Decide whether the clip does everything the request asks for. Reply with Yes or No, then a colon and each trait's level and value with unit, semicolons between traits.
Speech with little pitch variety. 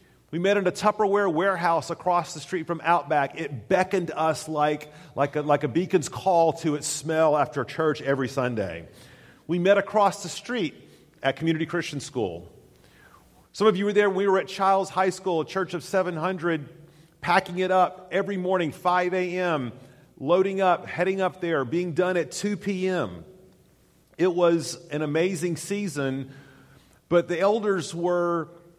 No: average, 3.3 semitones